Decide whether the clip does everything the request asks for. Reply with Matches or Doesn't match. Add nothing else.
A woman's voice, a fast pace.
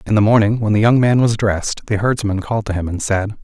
Doesn't match